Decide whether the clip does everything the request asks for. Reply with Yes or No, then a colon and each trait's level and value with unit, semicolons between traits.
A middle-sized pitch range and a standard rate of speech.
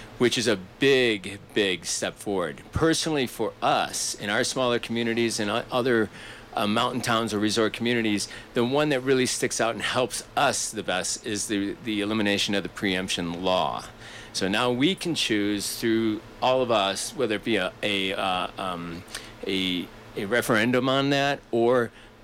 Yes: average, 3.3 semitones; average, 170 wpm